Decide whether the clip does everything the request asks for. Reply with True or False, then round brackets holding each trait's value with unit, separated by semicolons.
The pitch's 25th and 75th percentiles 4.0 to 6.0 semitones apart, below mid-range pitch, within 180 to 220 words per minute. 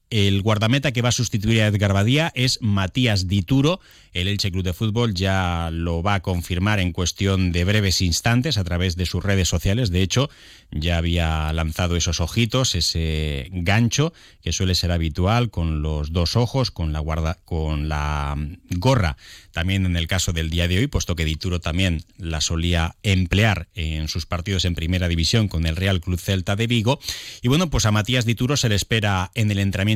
True (4.5 semitones; 95 Hz; 190 wpm)